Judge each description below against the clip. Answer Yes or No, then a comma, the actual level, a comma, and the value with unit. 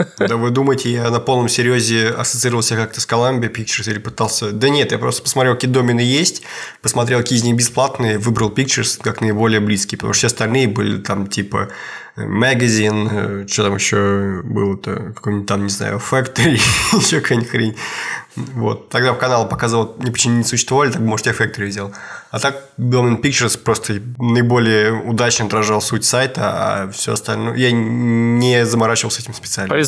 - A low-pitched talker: Yes, low, 115 Hz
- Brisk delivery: Yes, fast, 170 wpm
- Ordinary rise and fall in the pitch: No, narrow, 2.3 semitones